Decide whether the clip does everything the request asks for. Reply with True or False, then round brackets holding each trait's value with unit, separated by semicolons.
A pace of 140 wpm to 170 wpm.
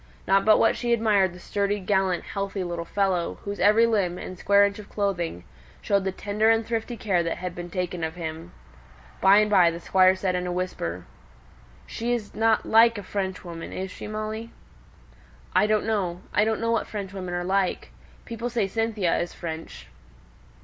False (185 wpm)